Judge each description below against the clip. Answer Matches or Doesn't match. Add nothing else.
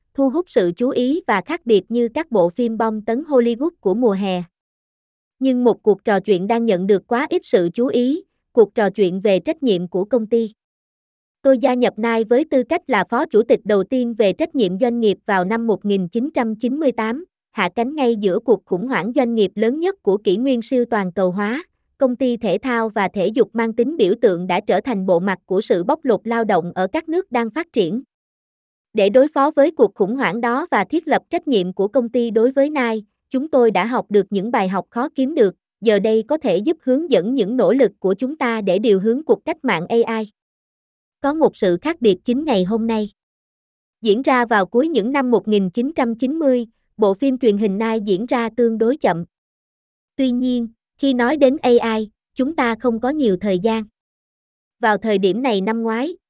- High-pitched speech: Matches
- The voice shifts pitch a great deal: Doesn't match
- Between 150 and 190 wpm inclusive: Doesn't match